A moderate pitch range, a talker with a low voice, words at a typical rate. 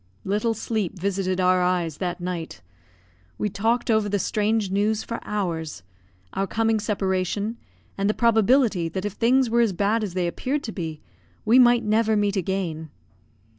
No: average, 3.4 semitones; high, 205 Hz; average, 165 wpm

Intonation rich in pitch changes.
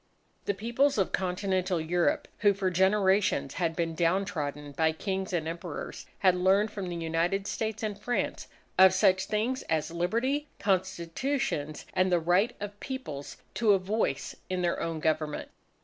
No: average, 3.6 semitones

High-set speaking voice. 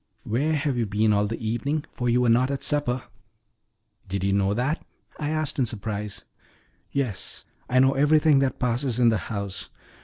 No: low, 125 Hz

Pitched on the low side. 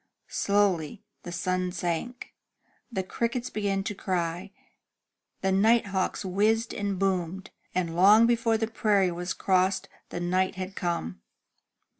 No: high, 190 Hz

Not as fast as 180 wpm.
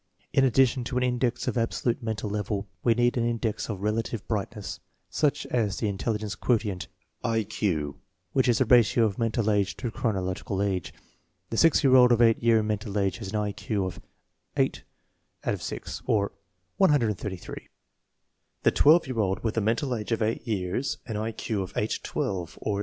No: average, 185 wpm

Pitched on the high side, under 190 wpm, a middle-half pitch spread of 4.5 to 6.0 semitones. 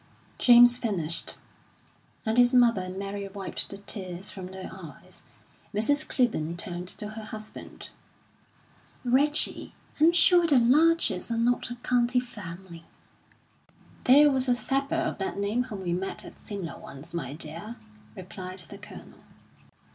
Yes: high, 215 Hz; average, 140 wpm; average, 5.2 semitones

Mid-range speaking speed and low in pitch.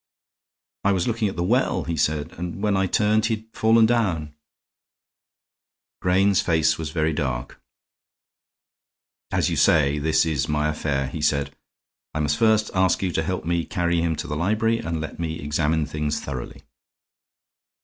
Yes: average, 165 wpm; very low, 80 Hz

